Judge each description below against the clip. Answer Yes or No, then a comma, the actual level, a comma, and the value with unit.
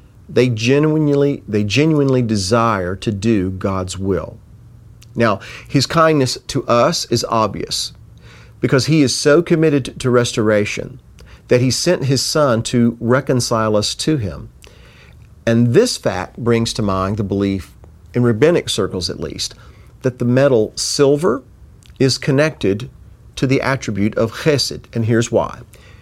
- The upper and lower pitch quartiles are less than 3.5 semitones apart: No, average, 4.1 semitones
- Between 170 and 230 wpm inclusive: No, average, 140 wpm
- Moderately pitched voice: No, low, 120 Hz